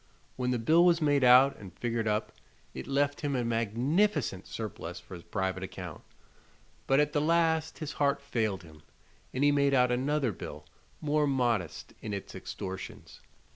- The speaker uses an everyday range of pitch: No, wide, 6.2 semitones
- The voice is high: No, low, 125 Hz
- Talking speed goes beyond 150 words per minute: Yes, average, 170 wpm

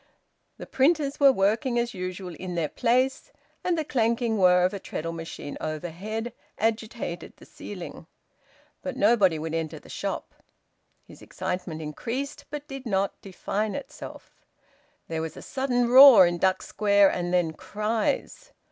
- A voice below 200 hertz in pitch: No, high, 205 Hz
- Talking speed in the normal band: Yes, average, 150 wpm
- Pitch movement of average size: No, wide, 5.7 semitones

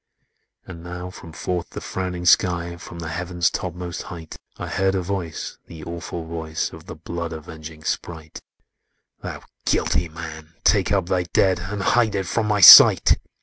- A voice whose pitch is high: No, very low, 85 Hz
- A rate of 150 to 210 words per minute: Yes, average, 160 wpm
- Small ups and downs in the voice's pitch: Yes, narrow, 1.9 semitones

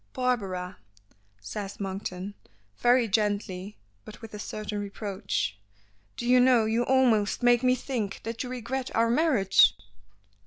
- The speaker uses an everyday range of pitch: Yes, average, 3.7 semitones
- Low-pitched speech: No, high, 220 Hz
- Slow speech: Yes, slow, 130 wpm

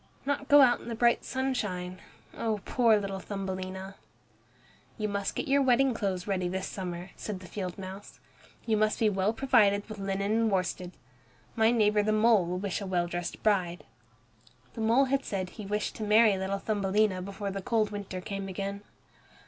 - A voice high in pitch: Yes, high, 200 Hz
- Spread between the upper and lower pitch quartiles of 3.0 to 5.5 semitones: No, narrow, 2.6 semitones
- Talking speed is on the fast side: No, average, 180 wpm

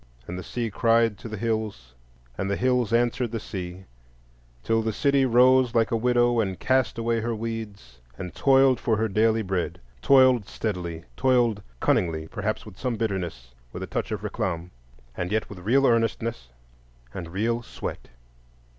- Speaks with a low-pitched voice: Yes, low, 110 Hz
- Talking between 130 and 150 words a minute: No, average, 160 wpm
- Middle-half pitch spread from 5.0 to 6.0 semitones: No, average, 4.2 semitones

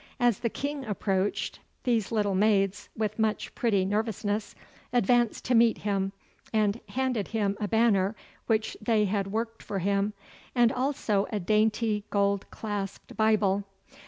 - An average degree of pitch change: No, narrow, 2.2 semitones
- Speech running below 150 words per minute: Yes, average, 140 wpm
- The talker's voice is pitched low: No, high, 215 Hz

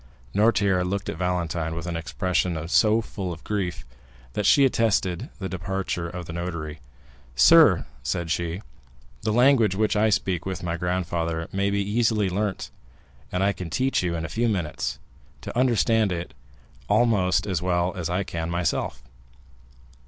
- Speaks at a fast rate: No, average, 160 wpm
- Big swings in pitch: No, average, 3.4 semitones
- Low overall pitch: Yes, very low, 90 Hz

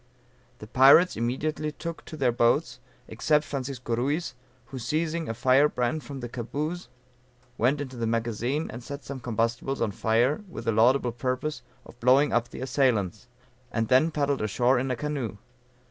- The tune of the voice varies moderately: Yes, average, 3.5 semitones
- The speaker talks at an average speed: Yes, average, 165 wpm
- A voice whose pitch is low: Yes, low, 130 Hz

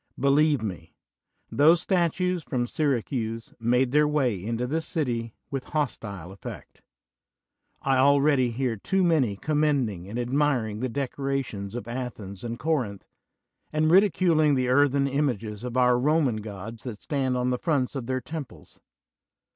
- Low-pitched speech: Yes, low, 130 Hz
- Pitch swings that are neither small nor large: Yes, average, 4.3 semitones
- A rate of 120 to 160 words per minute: Yes, average, 145 wpm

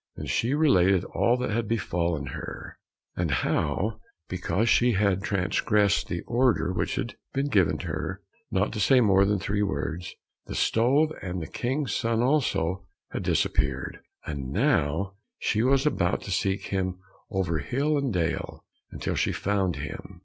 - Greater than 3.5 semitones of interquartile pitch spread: Yes, average, 5.0 semitones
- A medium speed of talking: Yes, average, 155 wpm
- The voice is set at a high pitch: No, low, 100 Hz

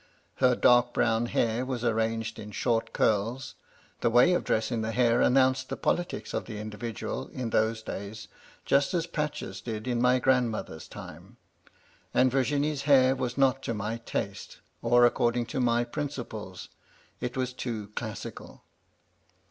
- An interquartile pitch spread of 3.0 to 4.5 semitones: No, narrow, 2.6 semitones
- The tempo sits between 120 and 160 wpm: Yes, average, 155 wpm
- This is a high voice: No, low, 120 Hz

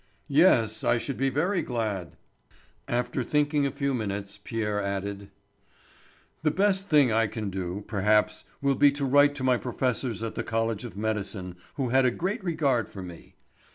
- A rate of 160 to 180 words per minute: Yes, average, 170 wpm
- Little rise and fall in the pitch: No, average, 5.2 semitones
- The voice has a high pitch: No, low, 120 Hz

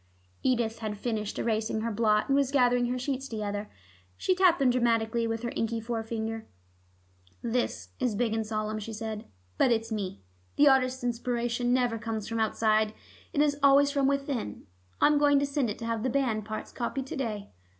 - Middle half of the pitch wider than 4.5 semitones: No, average, 3.0 semitones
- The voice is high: Yes, high, 230 Hz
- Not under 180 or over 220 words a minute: Yes, average, 185 wpm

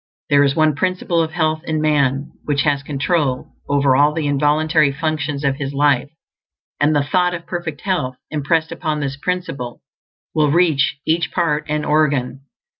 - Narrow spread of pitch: Yes, narrow, 2.2 semitones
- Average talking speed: Yes, average, 165 wpm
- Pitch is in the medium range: Yes, medium, 150 Hz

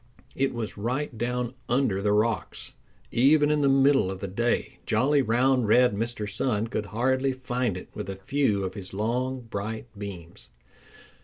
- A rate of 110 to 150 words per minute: No, average, 165 wpm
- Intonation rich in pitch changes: No, average, 4.2 semitones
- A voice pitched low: Yes, low, 120 Hz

